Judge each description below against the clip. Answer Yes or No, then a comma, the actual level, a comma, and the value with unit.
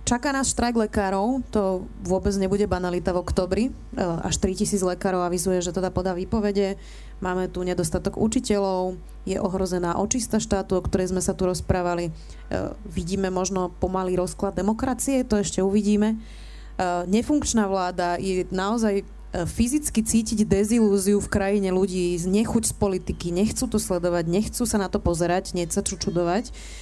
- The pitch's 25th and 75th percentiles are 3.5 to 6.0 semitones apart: No, narrow, 2.4 semitones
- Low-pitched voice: No, high, 195 Hz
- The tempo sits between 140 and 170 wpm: Yes, average, 150 wpm